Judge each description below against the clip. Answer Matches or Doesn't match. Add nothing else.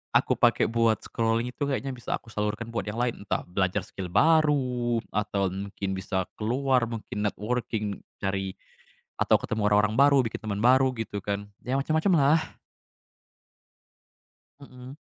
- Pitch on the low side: Matches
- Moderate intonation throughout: Matches